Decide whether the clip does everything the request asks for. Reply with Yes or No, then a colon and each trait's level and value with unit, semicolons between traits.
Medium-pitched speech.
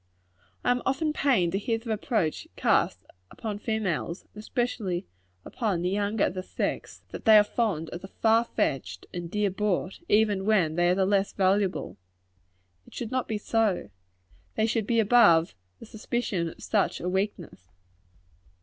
No: high, 205 Hz